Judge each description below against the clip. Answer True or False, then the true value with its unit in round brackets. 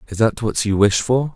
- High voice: False (110 Hz)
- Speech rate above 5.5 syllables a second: False (5.0 syllables/s)